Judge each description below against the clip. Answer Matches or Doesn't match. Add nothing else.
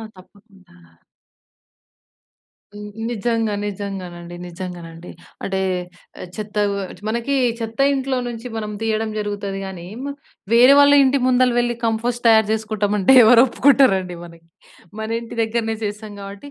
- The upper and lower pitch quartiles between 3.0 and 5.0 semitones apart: Matches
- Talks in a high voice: Matches